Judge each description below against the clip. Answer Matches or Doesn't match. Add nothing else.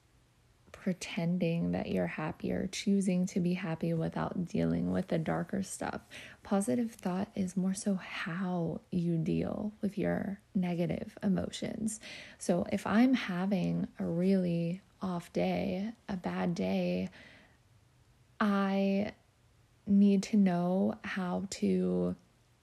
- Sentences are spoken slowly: Matches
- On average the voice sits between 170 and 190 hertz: Matches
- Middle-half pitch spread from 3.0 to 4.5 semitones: Matches